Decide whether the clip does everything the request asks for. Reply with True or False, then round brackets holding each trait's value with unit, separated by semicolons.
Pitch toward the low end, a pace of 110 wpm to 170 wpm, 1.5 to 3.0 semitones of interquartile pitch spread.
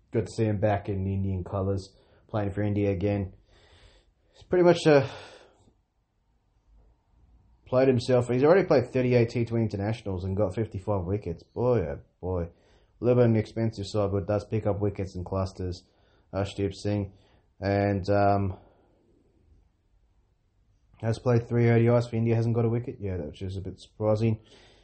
True (100 Hz; 160 wpm; 2.7 semitones)